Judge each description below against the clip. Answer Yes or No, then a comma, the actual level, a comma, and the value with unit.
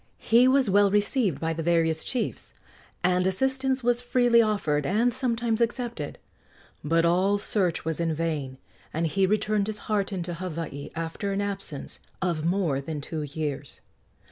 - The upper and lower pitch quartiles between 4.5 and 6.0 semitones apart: Yes, average, 5.3 semitones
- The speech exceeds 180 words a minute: No, average, 150 wpm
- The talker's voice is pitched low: No, high, 190 Hz